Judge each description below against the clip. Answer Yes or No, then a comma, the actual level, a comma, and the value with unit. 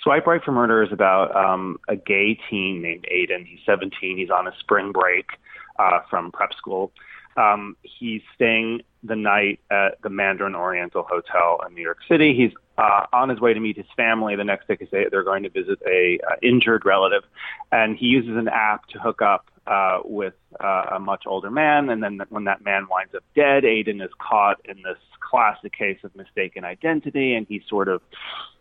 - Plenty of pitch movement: Yes, wide, 6.4 semitones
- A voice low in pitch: Yes, low, 110 Hz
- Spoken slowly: No, average, 195 wpm